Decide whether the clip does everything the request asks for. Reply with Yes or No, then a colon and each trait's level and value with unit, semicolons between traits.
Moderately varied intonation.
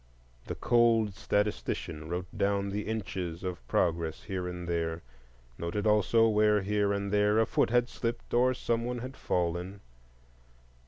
Yes: average, 4.1 semitones